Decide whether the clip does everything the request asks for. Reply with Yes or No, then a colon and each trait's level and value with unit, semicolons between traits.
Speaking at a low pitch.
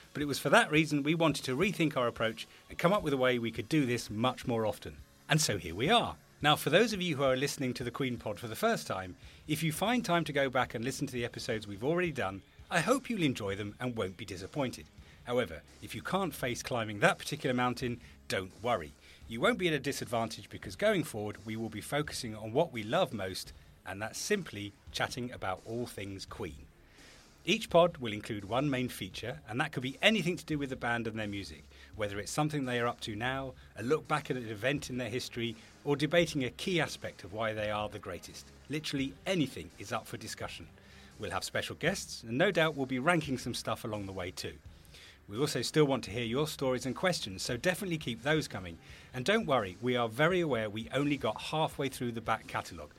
Yes: low, 125 Hz